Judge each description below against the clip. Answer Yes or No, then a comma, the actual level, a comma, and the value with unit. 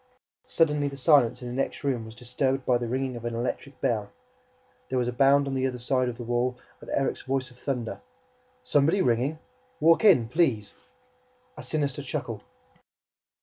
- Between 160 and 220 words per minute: Yes, average, 180 wpm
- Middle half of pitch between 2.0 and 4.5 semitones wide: Yes, narrow, 2.6 semitones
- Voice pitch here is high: No, low, 130 Hz